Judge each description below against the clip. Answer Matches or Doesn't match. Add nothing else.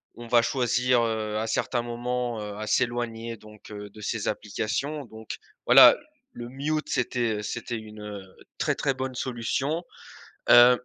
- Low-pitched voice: Matches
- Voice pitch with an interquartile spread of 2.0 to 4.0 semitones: Matches